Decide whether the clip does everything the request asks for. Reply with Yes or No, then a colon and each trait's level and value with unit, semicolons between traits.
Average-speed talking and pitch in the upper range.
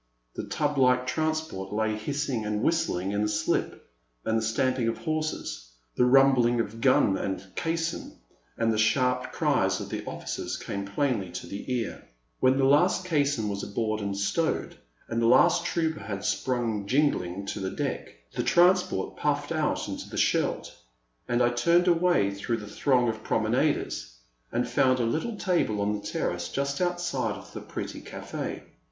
No: average, 170 wpm; low, 120 Hz